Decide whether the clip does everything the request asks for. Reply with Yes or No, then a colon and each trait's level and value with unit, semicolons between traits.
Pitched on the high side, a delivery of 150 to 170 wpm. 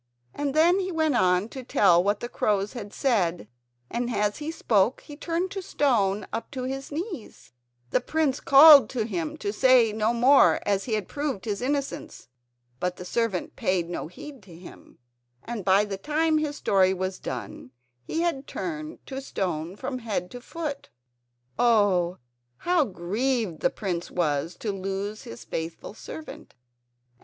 Yes: high, 225 Hz; average, 165 wpm